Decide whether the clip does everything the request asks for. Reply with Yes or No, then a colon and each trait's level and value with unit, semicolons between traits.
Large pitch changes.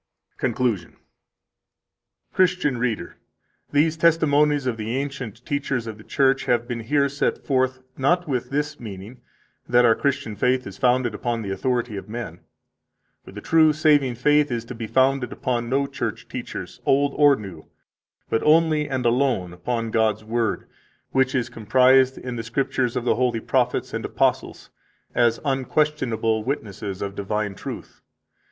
No: average, 3.7 semitones